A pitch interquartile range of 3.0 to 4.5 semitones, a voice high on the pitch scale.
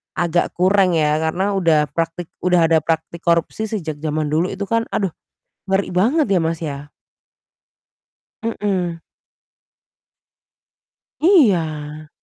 No: average, 3.7 semitones; medium, 170 Hz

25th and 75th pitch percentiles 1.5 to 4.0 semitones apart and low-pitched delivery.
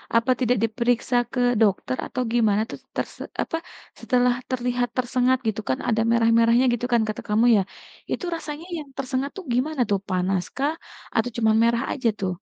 No: narrow, 2.6 semitones; high, 240 Hz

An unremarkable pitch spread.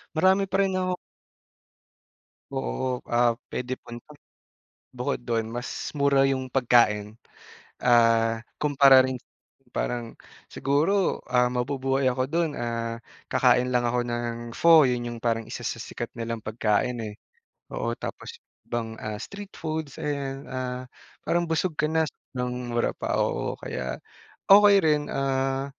Yes: average, 4.0 semitones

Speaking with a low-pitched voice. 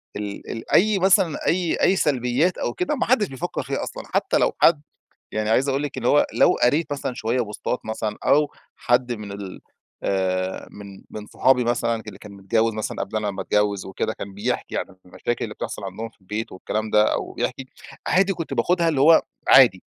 Yes: low, 115 Hz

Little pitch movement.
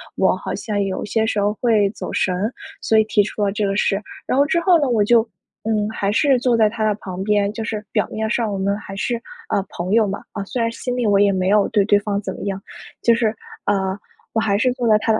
Yes: narrow, 2.2 semitones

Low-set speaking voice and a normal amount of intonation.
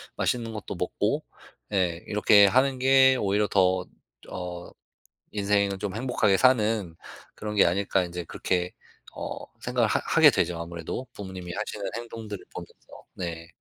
Yes: low, 100 Hz; average, 3.7 semitones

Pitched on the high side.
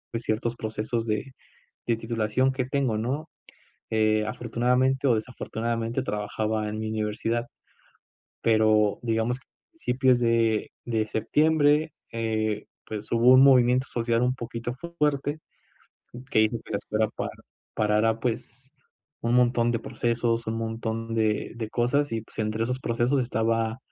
No: low, 115 Hz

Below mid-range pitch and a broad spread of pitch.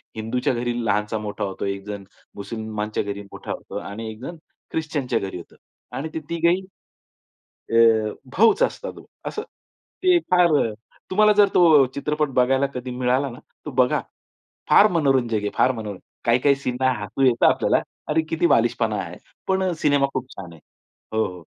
Yes: low, 125 Hz; wide, 6.2 semitones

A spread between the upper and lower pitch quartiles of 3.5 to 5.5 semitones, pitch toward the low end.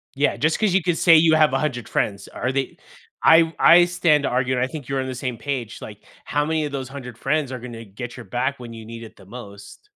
Yes: average, 4.4 semitones; low, 130 Hz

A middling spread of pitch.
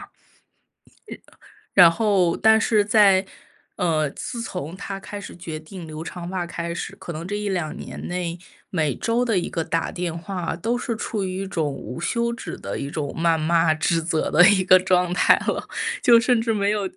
Yes: average, 3.7 semitones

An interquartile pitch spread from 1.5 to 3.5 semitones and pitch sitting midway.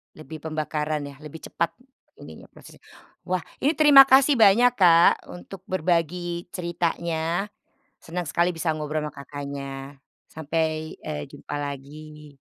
Yes: average, 2.8 semitones; medium, 160 Hz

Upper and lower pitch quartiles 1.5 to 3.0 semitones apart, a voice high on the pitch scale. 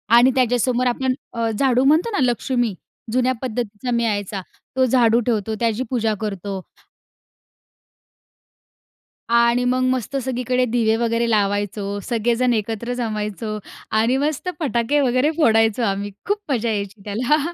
Yes: average, 2.7 semitones; high, 235 Hz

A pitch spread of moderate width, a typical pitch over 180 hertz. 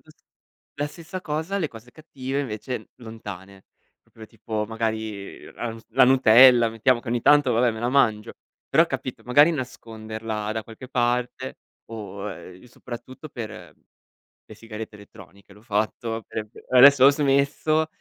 No: average, 3.4 semitones; low, 120 Hz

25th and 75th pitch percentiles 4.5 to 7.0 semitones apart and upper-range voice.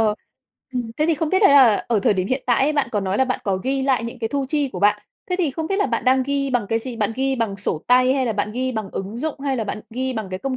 No: average, 4.0 semitones; very high, 255 Hz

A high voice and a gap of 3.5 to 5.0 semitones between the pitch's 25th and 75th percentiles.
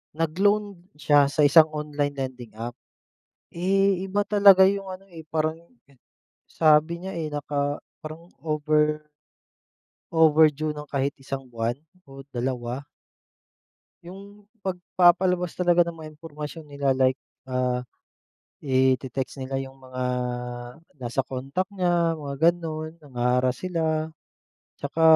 No: medium, 155 Hz; average, 4.4 semitones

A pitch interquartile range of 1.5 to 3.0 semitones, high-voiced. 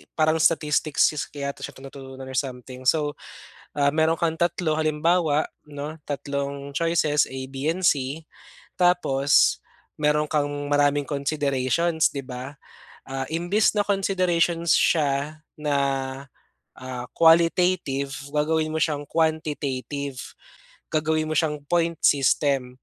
No: narrow, 2.6 semitones; medium, 150 Hz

